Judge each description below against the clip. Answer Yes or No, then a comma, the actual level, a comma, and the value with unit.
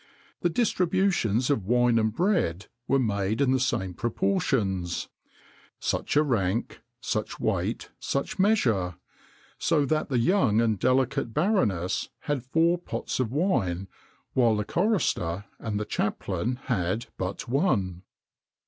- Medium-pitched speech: No, low, 120 Hz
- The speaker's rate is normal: No, slow, 130 wpm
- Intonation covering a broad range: Yes, wide, 7.5 semitones